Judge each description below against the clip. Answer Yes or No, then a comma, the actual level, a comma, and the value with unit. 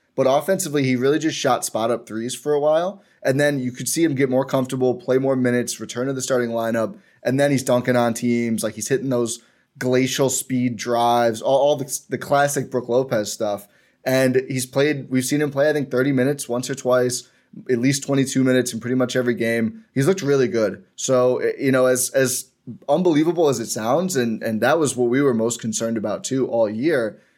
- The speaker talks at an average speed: No, fast, 215 wpm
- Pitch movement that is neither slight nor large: No, narrow, 2.3 semitones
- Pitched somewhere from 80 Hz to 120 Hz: No, low, 130 Hz